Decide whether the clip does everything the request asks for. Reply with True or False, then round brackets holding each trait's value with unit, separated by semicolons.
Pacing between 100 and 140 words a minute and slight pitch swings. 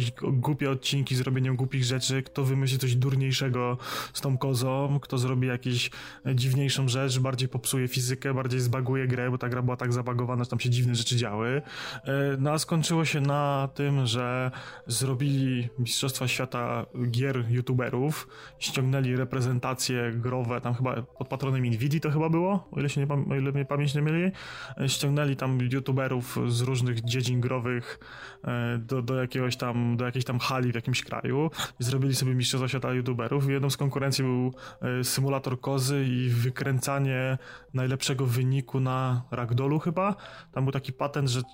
False (155 wpm; 1.5 semitones)